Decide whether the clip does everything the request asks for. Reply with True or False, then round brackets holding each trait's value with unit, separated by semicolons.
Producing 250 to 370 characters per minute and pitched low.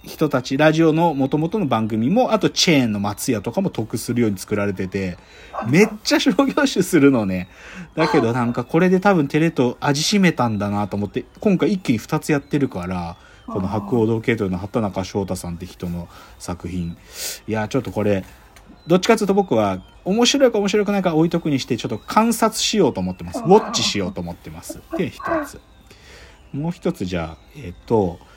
False (390 characters per minute; 125 Hz)